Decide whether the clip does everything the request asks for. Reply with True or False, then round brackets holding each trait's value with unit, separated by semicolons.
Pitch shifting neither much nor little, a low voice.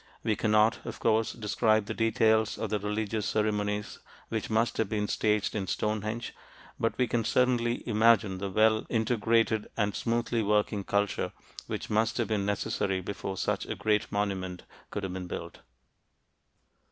False (1.6 semitones; 110 Hz)